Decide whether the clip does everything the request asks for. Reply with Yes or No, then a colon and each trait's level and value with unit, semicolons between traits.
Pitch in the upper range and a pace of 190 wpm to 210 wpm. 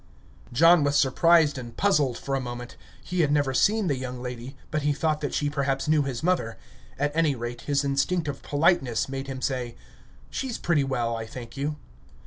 No: medium, 140 Hz; average, 195 wpm